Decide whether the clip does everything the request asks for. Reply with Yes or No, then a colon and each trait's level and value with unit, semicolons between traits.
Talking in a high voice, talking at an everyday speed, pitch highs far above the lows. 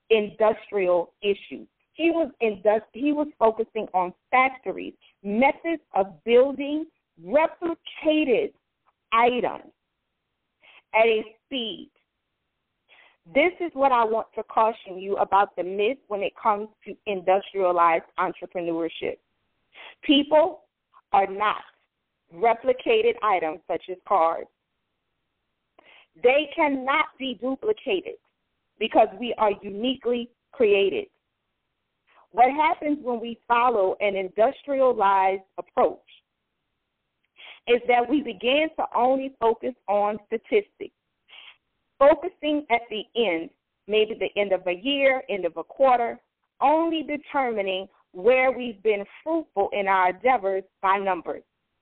No: high, 230 Hz; slow, 110 wpm; wide, 6.0 semitones